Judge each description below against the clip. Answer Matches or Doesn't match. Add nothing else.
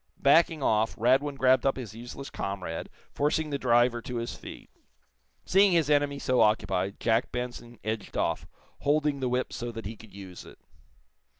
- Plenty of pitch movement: Doesn't match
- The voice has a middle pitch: Doesn't match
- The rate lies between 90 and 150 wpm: Doesn't match